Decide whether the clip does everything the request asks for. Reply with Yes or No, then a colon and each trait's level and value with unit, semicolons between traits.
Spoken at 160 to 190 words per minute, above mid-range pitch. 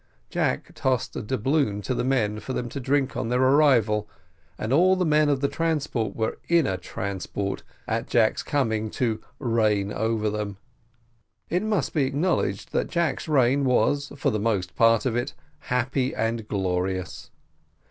No: average, 170 wpm; low, 120 Hz